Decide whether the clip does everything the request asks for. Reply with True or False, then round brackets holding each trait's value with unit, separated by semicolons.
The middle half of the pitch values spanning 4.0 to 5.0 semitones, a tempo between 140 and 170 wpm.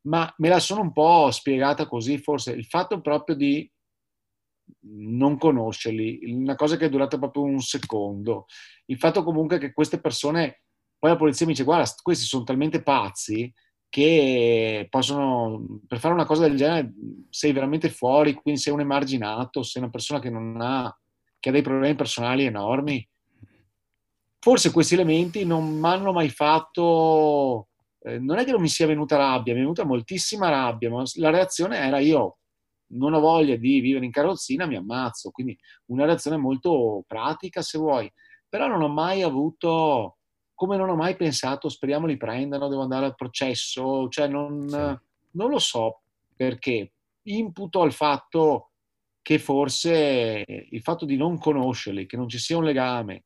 True (4.3 semitones; 165 wpm)